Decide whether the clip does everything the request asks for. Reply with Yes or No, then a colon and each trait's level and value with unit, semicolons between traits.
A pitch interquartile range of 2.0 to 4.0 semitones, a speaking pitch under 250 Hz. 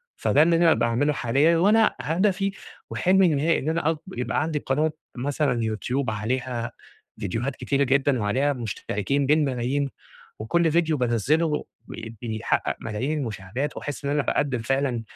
No: average, 4.6 semitones; medium, 140 Hz